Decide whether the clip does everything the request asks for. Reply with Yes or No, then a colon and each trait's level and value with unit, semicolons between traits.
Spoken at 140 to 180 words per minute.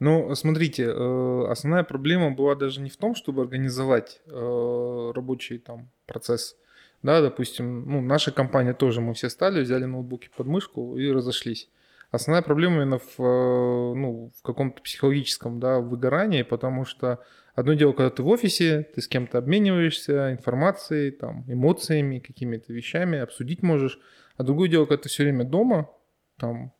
Yes: average, 150 wpm